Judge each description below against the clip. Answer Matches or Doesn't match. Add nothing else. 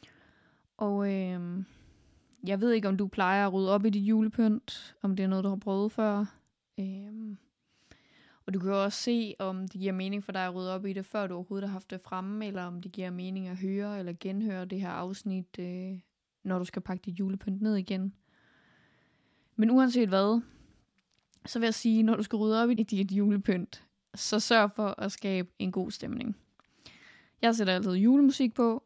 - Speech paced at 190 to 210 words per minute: Matches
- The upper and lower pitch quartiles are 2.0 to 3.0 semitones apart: Matches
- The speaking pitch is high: Matches